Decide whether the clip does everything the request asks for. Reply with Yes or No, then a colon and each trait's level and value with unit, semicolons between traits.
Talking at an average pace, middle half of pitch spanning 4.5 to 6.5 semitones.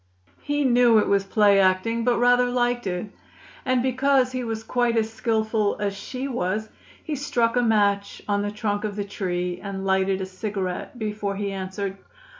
No: average, 180 wpm; average, 3.6 semitones